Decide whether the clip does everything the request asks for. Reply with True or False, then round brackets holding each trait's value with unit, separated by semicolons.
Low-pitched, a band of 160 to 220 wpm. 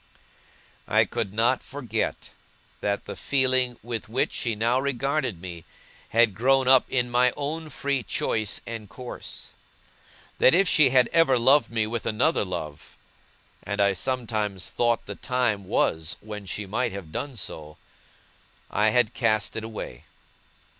False (115 Hz; 145 wpm)